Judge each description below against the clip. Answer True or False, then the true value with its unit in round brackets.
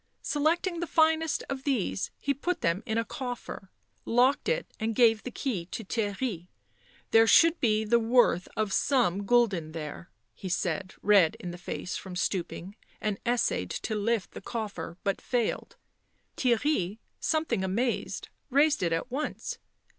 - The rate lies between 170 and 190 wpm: False (155 wpm)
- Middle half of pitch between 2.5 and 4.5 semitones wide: False (5.6 semitones)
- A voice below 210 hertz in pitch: False (225 Hz)